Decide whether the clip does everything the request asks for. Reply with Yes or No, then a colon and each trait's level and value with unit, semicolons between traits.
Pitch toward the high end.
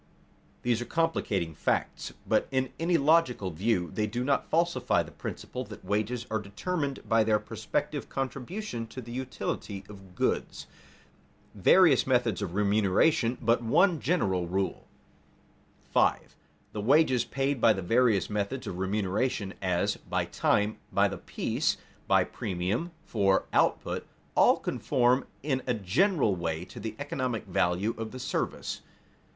No: low, 115 Hz